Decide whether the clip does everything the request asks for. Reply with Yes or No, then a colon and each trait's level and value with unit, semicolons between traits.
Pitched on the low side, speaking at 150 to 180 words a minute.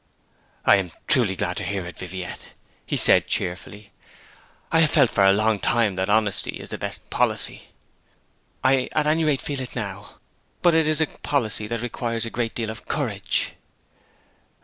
Yes: low, 110 Hz; average, 175 wpm